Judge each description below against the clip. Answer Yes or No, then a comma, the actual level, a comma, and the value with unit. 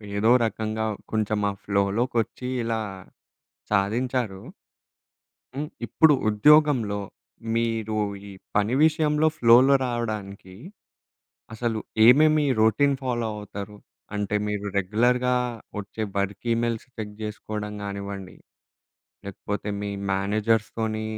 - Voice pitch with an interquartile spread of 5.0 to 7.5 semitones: No, average, 3.0 semitones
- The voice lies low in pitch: Yes, low, 110 Hz